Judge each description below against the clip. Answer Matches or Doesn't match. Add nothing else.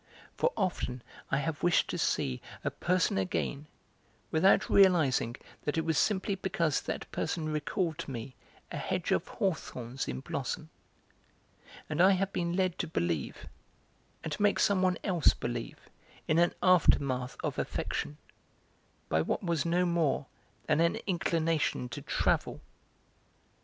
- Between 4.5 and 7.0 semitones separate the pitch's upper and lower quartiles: Matches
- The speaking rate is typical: Matches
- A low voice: Doesn't match